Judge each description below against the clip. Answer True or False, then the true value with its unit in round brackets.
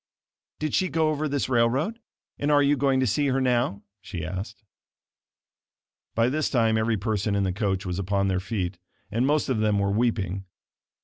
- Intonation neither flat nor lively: False (5.7 semitones)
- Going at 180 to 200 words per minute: True (185 wpm)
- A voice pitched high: False (115 Hz)